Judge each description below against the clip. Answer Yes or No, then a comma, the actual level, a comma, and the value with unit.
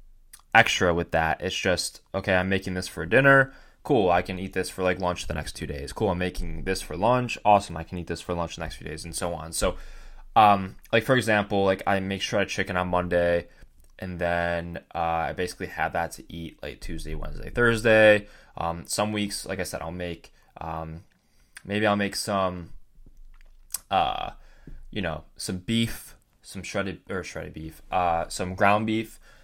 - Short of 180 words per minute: No, average, 195 wpm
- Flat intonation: No, average, 3.3 semitones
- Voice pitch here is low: Yes, very low, 90 Hz